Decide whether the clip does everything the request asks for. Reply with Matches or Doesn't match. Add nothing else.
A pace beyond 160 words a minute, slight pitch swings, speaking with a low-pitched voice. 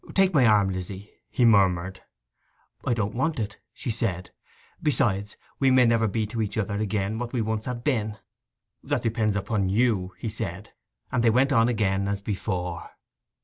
Doesn't match